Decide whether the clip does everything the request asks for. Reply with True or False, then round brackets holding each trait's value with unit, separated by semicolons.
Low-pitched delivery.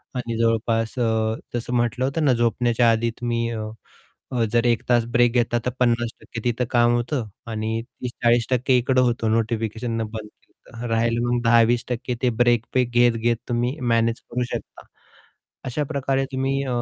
True (120 Hz)